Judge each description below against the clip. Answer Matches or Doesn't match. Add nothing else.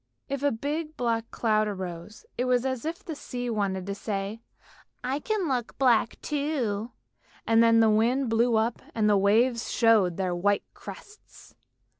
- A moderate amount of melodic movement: Matches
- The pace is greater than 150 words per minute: Matches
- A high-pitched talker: Matches